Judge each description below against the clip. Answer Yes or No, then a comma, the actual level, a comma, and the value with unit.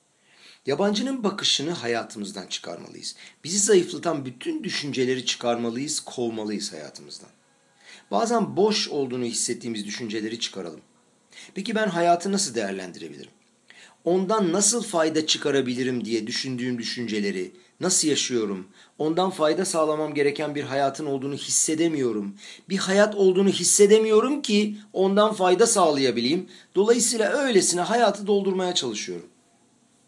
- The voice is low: No, medium, 155 Hz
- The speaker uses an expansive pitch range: Yes, wide, 8.7 semitones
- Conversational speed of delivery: Yes, average, 105 wpm